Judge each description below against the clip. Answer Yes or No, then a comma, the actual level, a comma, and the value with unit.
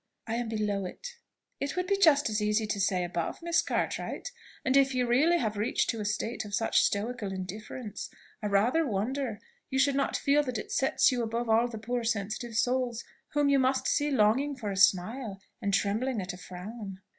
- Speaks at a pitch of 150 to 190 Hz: No, high, 230 Hz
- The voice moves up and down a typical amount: Yes, average, 4.4 semitones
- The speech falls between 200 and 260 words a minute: Yes, fast, 205 wpm